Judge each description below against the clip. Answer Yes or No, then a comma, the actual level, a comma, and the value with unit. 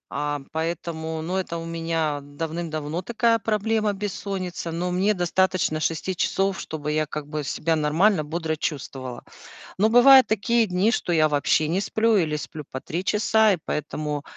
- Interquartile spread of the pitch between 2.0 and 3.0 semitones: No, average, 4.4 semitones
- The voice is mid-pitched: Yes, medium, 170 Hz